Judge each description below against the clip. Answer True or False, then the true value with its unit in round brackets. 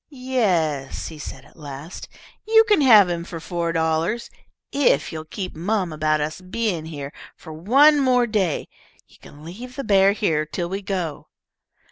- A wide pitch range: True (6.6 semitones)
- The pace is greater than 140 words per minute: True (165 wpm)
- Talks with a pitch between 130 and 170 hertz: False (180 Hz)